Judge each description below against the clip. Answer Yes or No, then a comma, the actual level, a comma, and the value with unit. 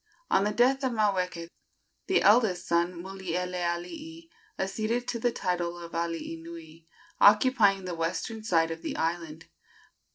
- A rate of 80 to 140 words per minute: Yes, slow, 135 wpm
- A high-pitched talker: No, medium, 180 Hz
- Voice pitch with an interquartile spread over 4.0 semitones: Yes, average, 4.4 semitones